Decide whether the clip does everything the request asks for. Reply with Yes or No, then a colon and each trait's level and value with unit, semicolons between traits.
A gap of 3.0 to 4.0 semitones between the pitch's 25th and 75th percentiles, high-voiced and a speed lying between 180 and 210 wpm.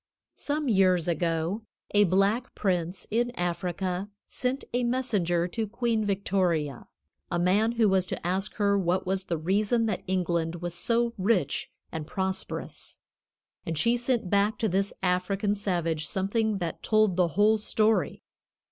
No: average, 3.6 semitones; high, 195 Hz; average, 145 wpm